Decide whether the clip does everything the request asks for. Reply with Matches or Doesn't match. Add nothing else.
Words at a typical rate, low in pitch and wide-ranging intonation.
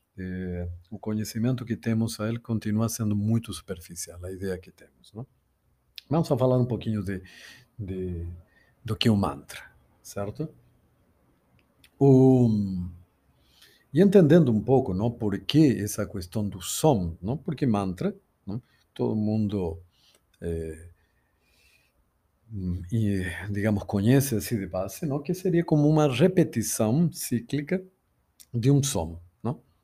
Matches